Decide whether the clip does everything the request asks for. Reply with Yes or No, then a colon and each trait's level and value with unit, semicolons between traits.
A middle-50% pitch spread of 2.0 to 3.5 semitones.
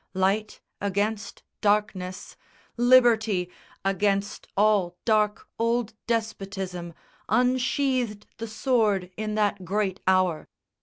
Yes: average, 2.7 semitones